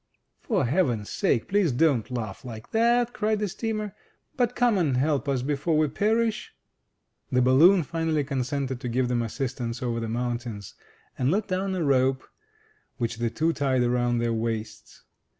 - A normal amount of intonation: No, wide, 7.1 semitones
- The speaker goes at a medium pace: Yes, average, 165 wpm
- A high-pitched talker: No, low, 135 Hz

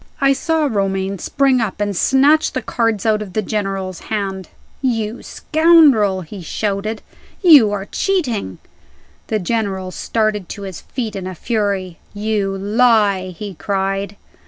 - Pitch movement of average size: Yes, average, 3.2 semitones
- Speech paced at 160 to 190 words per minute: No, average, 140 wpm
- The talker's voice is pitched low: No, high, 210 Hz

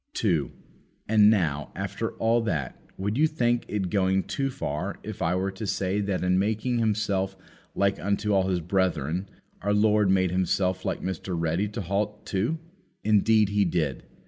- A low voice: Yes, low, 100 Hz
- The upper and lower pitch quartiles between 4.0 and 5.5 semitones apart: No, narrow, 2.5 semitones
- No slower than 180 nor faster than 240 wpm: No, average, 170 wpm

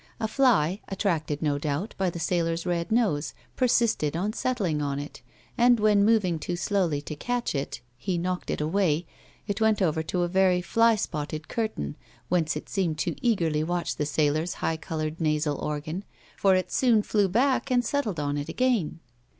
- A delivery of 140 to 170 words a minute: No, average, 180 wpm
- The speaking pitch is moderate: Yes, medium, 175 Hz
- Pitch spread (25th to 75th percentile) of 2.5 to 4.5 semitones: No, wide, 5.6 semitones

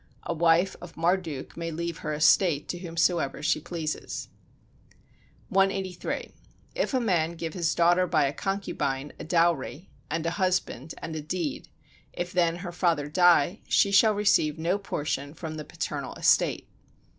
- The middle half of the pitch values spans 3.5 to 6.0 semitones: No, average, 2.7 semitones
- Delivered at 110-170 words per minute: Yes, average, 155 wpm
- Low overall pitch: No, medium, 170 Hz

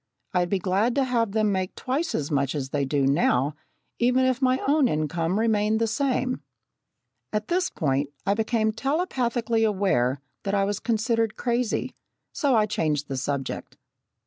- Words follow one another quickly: No, average, 165 wpm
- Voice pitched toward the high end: Yes, high, 215 Hz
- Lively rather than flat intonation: Yes, wide, 7.7 semitones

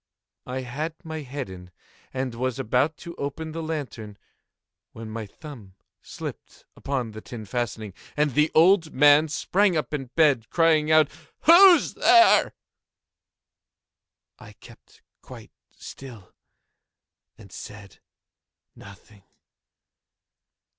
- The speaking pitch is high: No, medium, 140 Hz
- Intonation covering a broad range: Yes, wide, 5.8 semitones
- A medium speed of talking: No, slow, 110 wpm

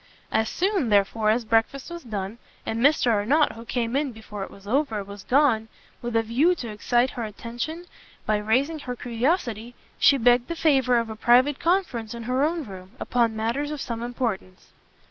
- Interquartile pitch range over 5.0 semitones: No, average, 4.0 semitones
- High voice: Yes, high, 240 Hz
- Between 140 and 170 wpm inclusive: No, average, 185 wpm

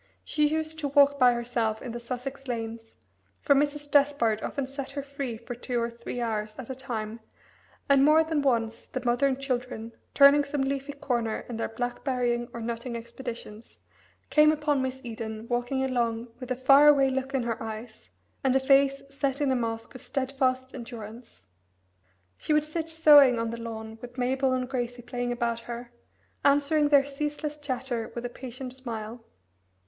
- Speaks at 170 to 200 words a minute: Yes, average, 180 wpm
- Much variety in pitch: No, average, 3.0 semitones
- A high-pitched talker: Yes, very high, 255 Hz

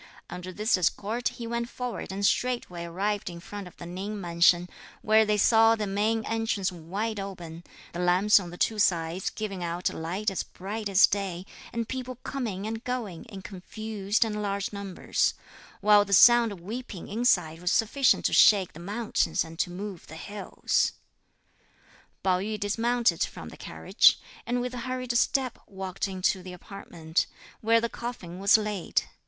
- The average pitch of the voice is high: Yes, high, 200 Hz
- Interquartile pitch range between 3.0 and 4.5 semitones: Yes, average, 3.7 semitones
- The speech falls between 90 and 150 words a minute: No, average, 170 wpm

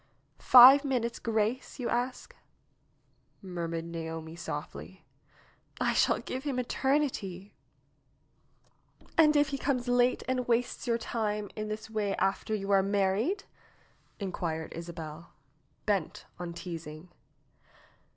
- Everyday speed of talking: No, slow, 115 wpm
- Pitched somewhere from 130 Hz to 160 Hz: No, high, 210 Hz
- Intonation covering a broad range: Yes, wide, 6.2 semitones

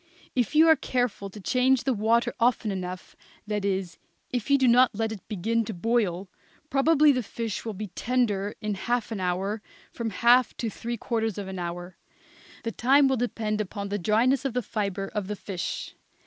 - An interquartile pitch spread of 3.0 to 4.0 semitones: Yes, average, 3.7 semitones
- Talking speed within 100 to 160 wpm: No, average, 190 wpm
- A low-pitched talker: No, high, 220 Hz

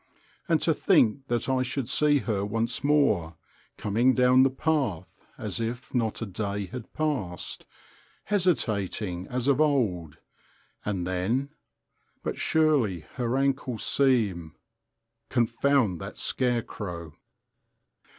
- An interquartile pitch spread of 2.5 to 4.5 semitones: No, average, 5.2 semitones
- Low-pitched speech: Yes, low, 120 Hz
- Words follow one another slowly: Yes, slow, 110 wpm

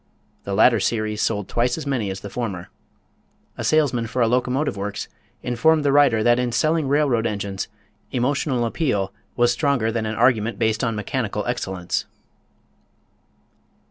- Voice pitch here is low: Yes, low, 120 Hz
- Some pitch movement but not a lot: Yes, average, 3.7 semitones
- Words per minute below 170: Yes, average, 150 wpm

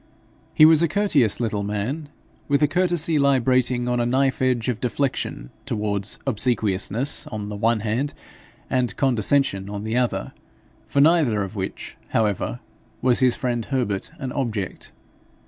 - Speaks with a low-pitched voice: Yes, low, 125 Hz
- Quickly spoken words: No, average, 145 wpm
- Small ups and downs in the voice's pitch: No, average, 4.6 semitones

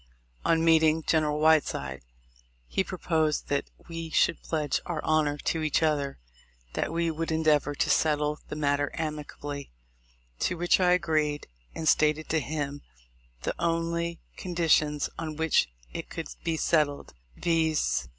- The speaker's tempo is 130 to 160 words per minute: Yes, average, 140 wpm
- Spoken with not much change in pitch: Yes, narrow, 1.8 semitones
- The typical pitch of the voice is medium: Yes, medium, 155 Hz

